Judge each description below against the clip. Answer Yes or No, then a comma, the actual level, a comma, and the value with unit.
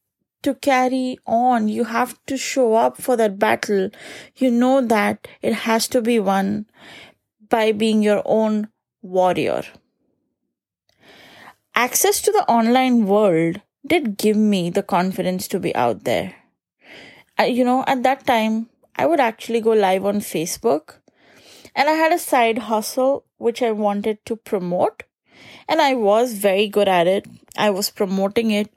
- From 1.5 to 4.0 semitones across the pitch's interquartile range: Yes, average, 3.6 semitones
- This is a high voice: Yes, high, 225 Hz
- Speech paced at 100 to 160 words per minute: Yes, average, 150 wpm